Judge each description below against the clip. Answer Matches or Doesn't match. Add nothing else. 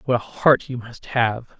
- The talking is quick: Matches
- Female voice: Doesn't match